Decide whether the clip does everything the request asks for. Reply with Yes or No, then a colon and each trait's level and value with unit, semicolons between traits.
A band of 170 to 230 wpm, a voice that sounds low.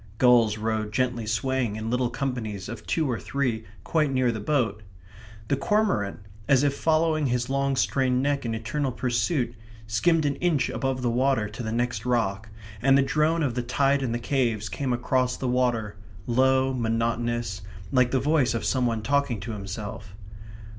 Yes: average, 175 wpm; low, 125 Hz